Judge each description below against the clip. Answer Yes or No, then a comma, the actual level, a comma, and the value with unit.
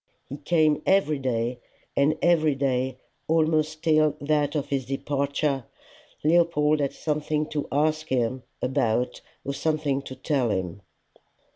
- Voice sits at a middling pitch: Yes, medium, 145 Hz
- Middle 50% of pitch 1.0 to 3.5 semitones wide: Yes, average, 2.7 semitones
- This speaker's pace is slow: Yes, slow, 130 wpm